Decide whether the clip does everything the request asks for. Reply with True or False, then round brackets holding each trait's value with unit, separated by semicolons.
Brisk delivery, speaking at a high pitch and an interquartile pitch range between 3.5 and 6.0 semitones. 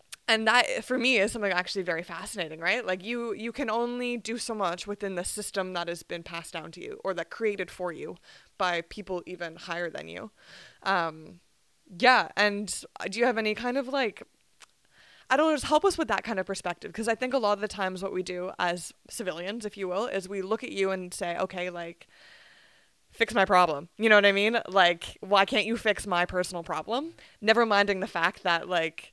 True (220 wpm; 195 Hz; 4.2 semitones)